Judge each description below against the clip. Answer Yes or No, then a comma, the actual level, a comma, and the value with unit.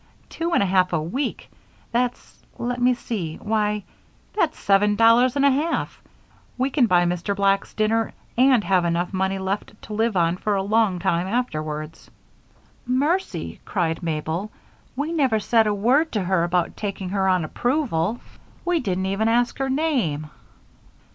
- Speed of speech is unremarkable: Yes, average, 160 wpm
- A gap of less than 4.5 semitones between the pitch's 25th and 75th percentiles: No, average, 5.3 semitones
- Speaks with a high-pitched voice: Yes, high, 210 Hz